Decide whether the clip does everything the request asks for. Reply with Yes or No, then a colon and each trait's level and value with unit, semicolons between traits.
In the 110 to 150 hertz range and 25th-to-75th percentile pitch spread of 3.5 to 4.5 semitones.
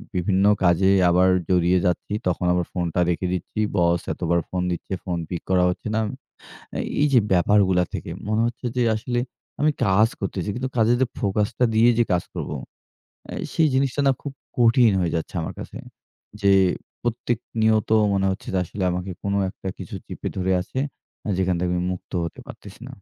No: very low, 95 Hz; average, 4.1 semitones